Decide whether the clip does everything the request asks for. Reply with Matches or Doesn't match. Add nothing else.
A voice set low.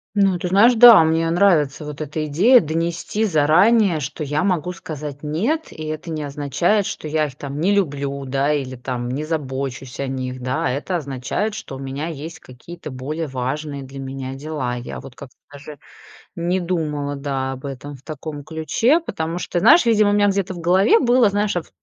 Doesn't match